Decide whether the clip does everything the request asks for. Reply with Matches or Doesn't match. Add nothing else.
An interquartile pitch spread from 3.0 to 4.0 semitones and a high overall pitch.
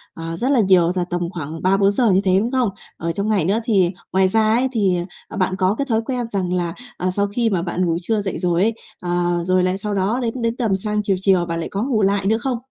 Matches